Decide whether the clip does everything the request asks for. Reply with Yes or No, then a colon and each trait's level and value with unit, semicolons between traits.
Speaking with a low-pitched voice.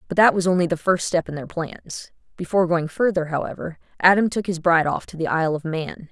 No: medium, 170 Hz